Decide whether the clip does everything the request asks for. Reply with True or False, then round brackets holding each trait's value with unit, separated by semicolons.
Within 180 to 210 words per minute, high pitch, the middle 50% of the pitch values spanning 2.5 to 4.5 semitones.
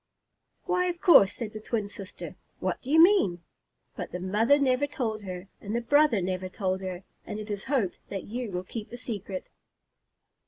False (190 wpm; 215 Hz; 5.3 semitones)